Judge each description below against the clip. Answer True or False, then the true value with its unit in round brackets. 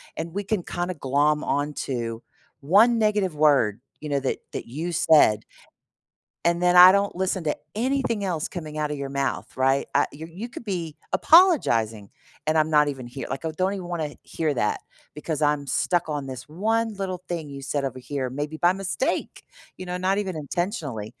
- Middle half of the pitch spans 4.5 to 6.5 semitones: True (4.9 semitones)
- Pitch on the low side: False (155 Hz)